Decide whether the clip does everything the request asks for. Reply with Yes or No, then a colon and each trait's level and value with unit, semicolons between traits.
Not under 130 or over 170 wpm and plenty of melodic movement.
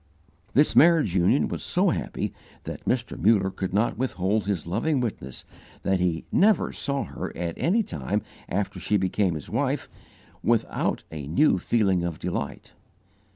Yes: average, 155 wpm; wide, 5.9 semitones